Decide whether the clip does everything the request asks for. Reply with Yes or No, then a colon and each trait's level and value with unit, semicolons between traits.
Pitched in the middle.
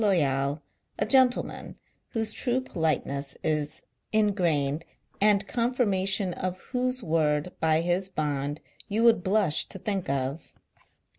Yes: medium, 180 Hz